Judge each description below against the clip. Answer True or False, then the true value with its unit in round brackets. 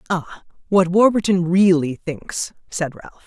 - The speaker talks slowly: True (130 wpm)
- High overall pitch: False (175 Hz)